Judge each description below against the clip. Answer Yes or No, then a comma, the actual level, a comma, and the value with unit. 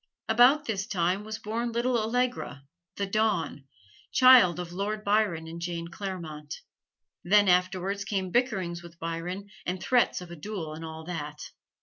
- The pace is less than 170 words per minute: Yes, average, 150 wpm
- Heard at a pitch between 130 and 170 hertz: No, high, 190 Hz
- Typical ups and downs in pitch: Yes, average, 4.2 semitones